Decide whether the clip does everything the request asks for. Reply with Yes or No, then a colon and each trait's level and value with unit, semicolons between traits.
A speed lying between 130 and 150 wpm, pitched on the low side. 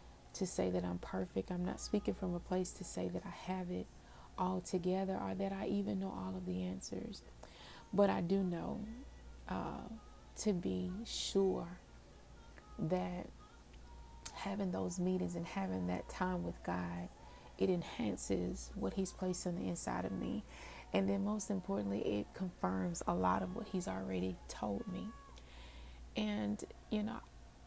No: average, 160 wpm; low, 105 Hz